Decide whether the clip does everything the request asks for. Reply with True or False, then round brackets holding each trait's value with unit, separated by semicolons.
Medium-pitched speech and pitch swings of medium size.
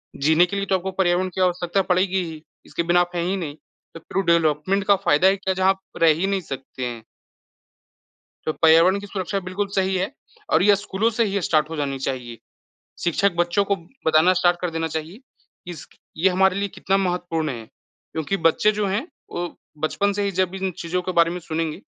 True (180 Hz; 3.0 semitones)